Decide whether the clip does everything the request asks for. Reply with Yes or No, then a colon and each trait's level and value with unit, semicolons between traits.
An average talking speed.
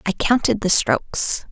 Yes: average, 160 wpm